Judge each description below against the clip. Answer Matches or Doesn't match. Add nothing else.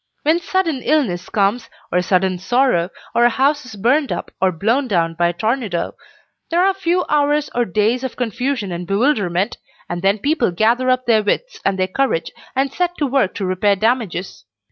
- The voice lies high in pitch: Matches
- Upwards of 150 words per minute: Matches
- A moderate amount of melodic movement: Doesn't match